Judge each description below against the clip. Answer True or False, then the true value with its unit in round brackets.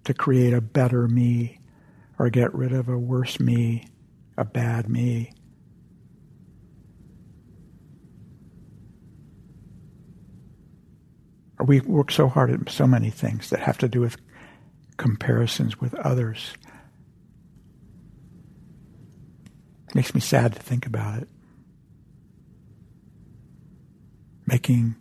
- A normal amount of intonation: False (1.8 semitones)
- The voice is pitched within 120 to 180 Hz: True (125 Hz)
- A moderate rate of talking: False (95 wpm)